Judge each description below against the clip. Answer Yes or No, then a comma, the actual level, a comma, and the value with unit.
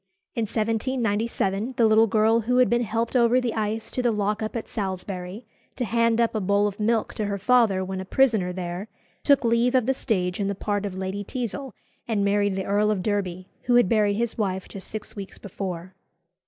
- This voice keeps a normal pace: No, fast, 210 wpm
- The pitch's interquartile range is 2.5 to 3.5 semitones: Yes, average, 2.9 semitones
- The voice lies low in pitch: No, high, 215 Hz